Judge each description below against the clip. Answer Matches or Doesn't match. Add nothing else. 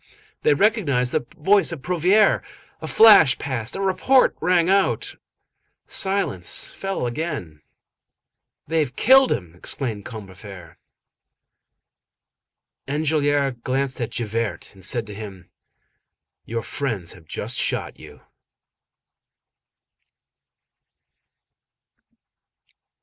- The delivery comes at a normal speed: Doesn't match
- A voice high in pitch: Doesn't match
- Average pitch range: Doesn't match